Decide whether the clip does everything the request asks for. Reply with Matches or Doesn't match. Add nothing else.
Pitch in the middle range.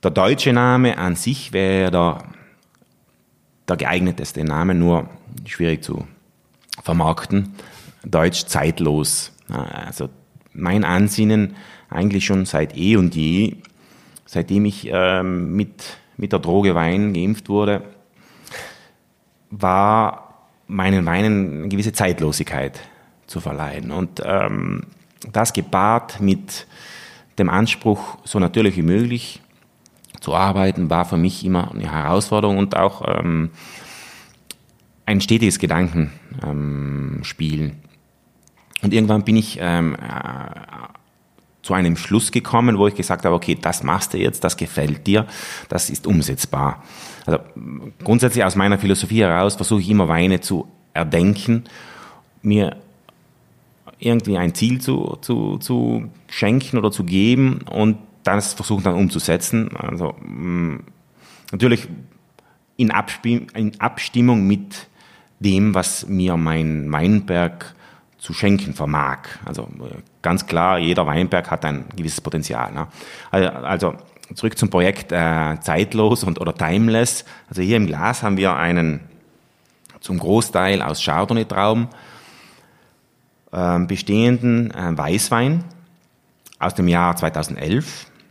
Doesn't match